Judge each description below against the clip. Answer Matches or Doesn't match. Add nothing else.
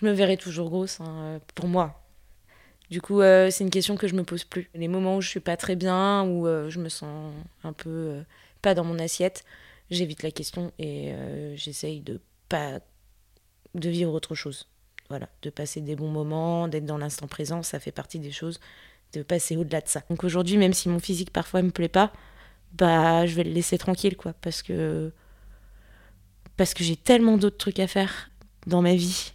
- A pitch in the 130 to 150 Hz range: Doesn't match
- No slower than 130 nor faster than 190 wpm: Doesn't match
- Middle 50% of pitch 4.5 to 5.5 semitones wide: Doesn't match